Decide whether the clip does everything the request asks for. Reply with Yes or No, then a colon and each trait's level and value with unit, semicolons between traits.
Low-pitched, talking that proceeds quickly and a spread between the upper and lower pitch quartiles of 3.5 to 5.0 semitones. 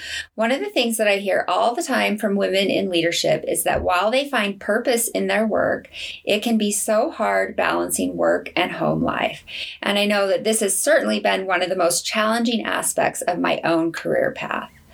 No: high, 200 Hz; fast, 210 wpm; average, 4.4 semitones